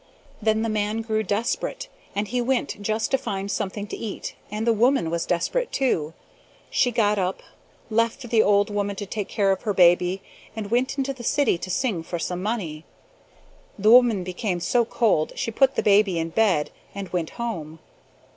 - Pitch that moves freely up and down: No, average, 3.8 semitones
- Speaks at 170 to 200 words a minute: Yes, average, 185 wpm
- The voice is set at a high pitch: Yes, high, 210 Hz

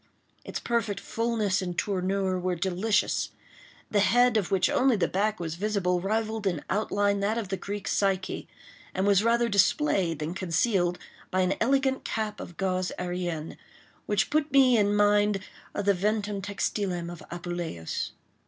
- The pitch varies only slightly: No, average, 3.0 semitones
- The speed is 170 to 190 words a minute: No, average, 155 wpm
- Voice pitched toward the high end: Yes, high, 200 Hz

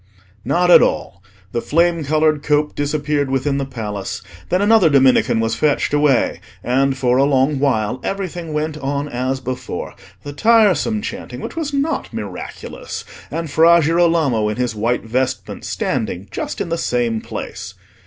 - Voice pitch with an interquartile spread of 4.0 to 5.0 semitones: Yes, average, 4.7 semitones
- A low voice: No, medium, 145 Hz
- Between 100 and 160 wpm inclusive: Yes, average, 155 wpm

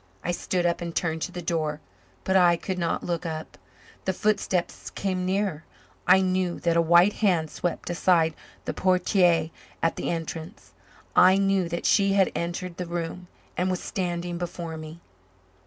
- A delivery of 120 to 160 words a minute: No, average, 170 wpm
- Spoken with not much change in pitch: Yes, narrow, 1.8 semitones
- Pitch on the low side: No, medium, 175 Hz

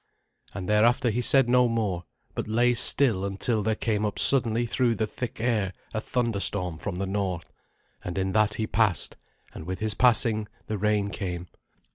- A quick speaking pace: No, average, 175 wpm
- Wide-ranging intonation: No, average, 3.2 semitones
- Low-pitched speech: Yes, low, 110 Hz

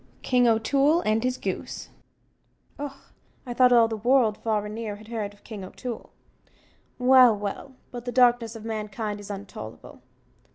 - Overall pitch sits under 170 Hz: No, high, 225 Hz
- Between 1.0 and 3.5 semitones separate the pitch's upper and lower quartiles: Yes, average, 3.0 semitones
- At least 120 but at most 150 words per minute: No, average, 160 wpm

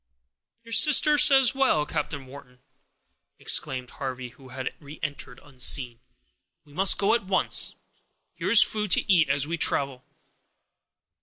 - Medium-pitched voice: Yes, medium, 145 Hz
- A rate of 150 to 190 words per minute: No, slow, 135 wpm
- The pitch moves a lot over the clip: Yes, wide, 7.5 semitones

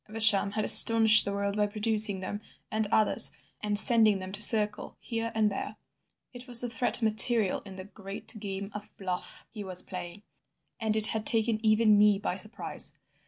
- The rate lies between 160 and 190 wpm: Yes, average, 180 wpm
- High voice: Yes, high, 210 Hz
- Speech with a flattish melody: Yes, narrow, 1.8 semitones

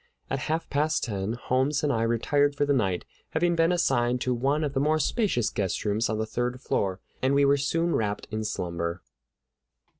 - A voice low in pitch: Yes, low, 130 Hz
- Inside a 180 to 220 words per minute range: Yes, average, 190 wpm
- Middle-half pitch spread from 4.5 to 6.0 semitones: Yes, average, 5.2 semitones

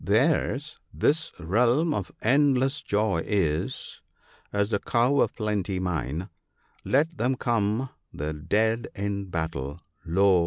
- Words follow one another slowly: Yes, slow, 125 wpm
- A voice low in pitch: Yes, low, 105 Hz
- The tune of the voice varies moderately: No, wide, 5.9 semitones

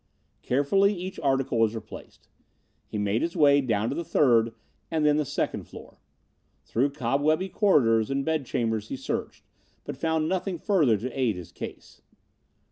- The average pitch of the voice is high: No, medium, 140 Hz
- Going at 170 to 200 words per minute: No, average, 155 wpm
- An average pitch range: No, wide, 5.7 semitones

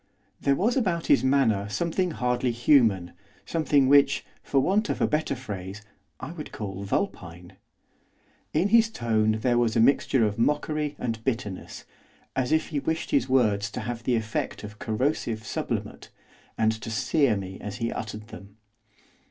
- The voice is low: Yes, low, 120 Hz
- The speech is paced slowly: No, average, 160 wpm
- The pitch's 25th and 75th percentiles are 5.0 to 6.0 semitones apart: Yes, wide, 5.5 semitones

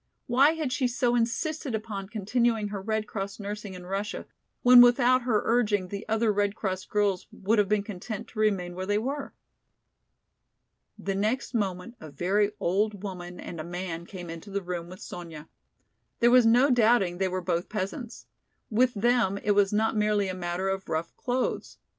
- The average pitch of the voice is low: No, high, 205 Hz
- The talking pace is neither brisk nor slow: Yes, average, 180 wpm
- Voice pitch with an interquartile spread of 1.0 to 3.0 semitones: No, average, 3.9 semitones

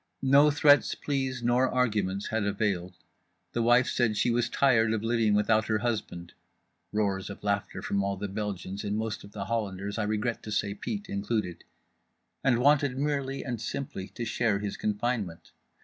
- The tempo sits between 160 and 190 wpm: Yes, average, 165 wpm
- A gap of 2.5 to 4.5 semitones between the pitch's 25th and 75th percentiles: Yes, average, 3.2 semitones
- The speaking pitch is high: No, low, 110 Hz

